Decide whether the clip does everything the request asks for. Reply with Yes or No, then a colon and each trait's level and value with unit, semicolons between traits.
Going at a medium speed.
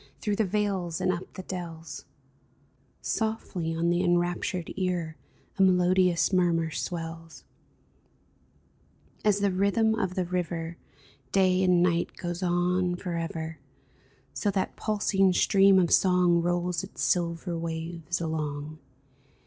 No: slow, 125 wpm